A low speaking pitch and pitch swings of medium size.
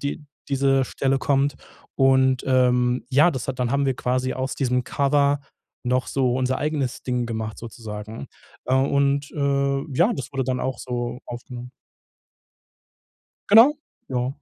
No: low, 130 Hz; narrow, 1.9 semitones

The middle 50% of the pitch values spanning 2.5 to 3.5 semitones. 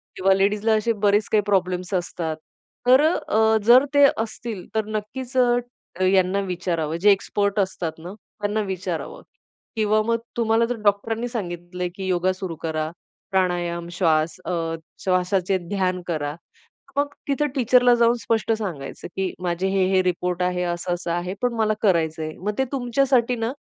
No: average, 4.0 semitones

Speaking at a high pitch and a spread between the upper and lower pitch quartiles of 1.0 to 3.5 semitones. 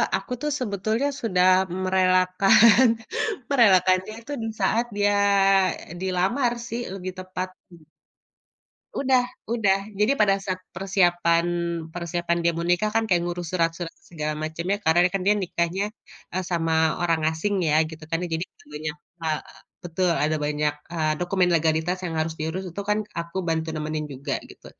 No: medium, 180 Hz; average, 3.2 semitones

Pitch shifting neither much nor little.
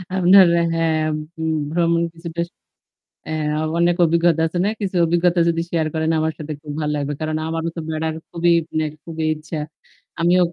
No: narrow, 1.5 semitones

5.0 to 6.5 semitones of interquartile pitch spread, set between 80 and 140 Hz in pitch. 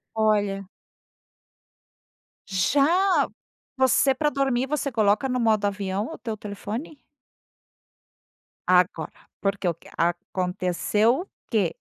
No: average, 5.3 semitones; high, 215 Hz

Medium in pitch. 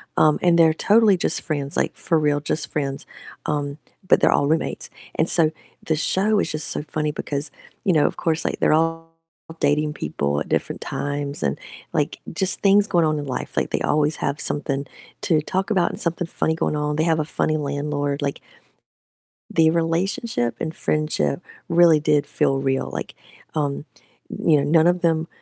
Yes: medium, 155 Hz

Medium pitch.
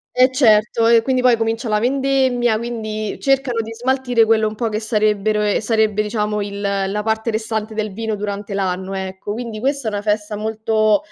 No: high, 220 Hz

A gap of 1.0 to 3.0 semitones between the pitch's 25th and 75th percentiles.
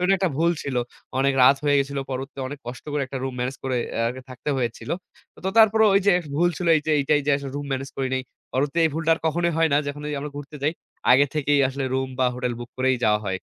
Yes: average, 2.7 semitones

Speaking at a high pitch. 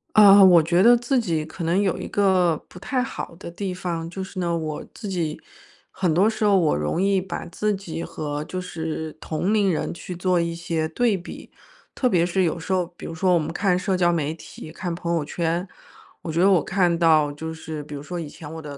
No: medium, 175 Hz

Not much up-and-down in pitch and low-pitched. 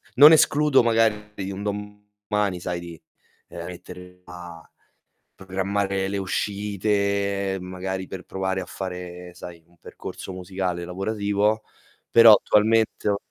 Yes: narrow, 2.3 semitones; very low, 95 Hz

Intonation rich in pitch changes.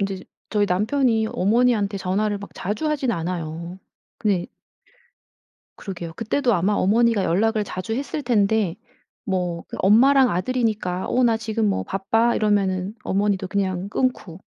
No: average, 3.5 semitones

